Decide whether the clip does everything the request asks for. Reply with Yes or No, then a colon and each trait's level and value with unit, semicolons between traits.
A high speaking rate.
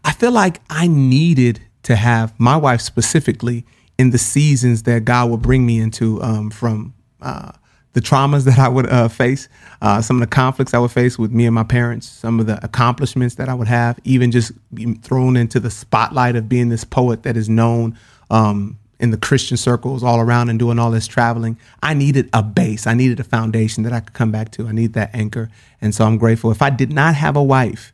Yes: fast, 225 wpm